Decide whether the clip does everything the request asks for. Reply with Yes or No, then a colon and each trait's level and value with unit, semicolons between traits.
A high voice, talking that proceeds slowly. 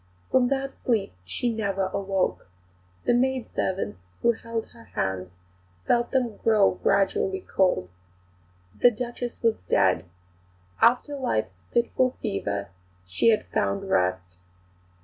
Yes: high, 215 Hz; slow, 115 wpm